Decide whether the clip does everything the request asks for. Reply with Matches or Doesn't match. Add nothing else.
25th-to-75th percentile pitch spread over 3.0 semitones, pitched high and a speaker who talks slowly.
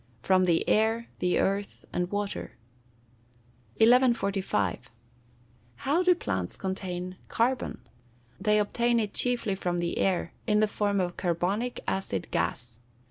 Matches